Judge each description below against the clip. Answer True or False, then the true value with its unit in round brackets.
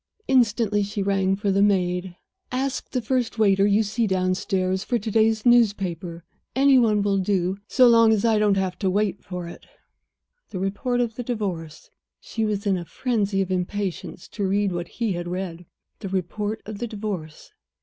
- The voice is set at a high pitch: True (200 Hz)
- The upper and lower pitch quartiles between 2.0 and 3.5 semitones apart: True (3.0 semitones)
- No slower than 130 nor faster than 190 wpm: True (170 wpm)